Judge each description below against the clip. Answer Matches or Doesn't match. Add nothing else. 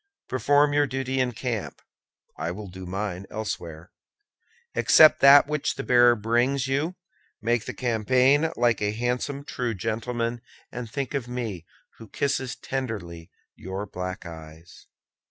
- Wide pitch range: Doesn't match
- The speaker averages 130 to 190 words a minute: Matches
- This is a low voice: Matches